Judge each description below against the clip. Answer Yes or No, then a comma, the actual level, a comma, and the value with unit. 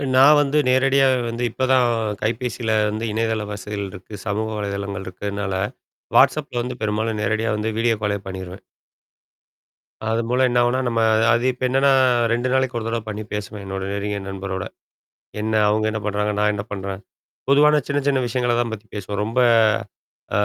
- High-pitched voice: No, low, 110 Hz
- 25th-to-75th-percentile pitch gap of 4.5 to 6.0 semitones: No, average, 3.3 semitones